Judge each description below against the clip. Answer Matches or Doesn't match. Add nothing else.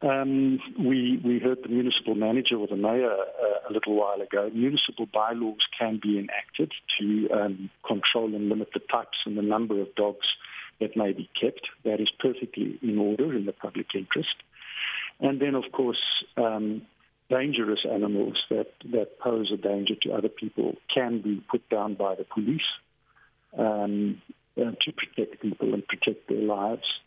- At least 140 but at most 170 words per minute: Matches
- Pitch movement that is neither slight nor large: Matches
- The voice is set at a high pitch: Doesn't match